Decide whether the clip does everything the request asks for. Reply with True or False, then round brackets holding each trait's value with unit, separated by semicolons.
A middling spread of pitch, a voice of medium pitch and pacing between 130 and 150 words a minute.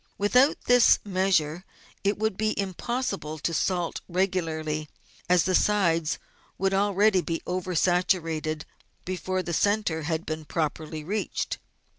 True (3.7 semitones; 180 Hz; 135 wpm)